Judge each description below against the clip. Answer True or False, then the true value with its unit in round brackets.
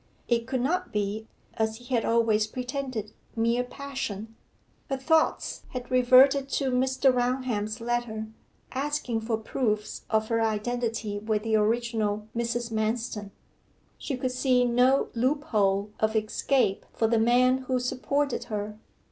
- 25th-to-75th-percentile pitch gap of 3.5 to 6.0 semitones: False (2.8 semitones)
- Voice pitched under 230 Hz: False (235 Hz)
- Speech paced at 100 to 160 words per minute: True (135 wpm)